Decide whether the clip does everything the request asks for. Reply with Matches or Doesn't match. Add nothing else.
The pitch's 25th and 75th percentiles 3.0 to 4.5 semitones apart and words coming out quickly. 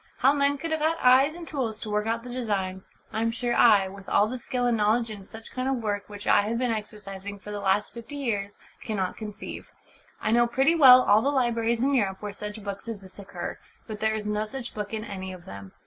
Matches